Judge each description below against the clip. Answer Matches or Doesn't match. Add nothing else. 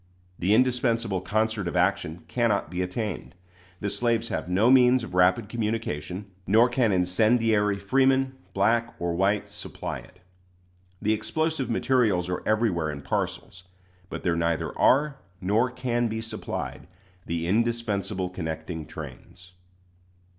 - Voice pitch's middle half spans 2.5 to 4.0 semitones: Doesn't match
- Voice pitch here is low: Matches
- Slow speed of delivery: Matches